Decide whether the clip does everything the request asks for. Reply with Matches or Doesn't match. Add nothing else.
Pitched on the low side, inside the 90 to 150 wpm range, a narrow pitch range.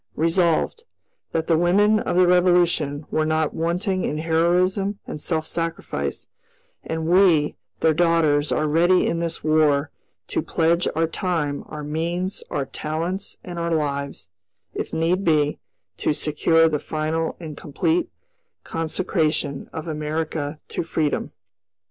Doesn't match